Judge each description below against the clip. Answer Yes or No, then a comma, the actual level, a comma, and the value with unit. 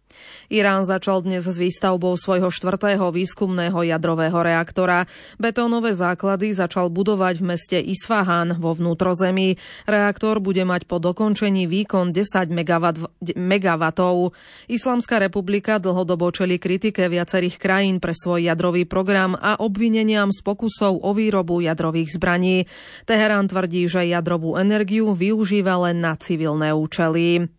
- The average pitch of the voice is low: No, medium, 185 Hz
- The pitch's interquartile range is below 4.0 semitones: Yes, narrow, 2.4 semitones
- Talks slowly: No, average, 120 wpm